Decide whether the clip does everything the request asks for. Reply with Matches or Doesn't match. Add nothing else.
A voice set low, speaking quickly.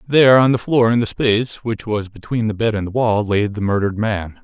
Matches